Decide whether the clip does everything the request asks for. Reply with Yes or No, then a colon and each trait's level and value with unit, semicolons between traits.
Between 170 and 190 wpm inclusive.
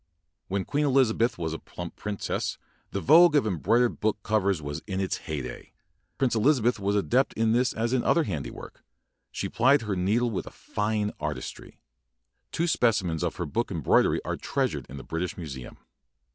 Yes: average, 175 wpm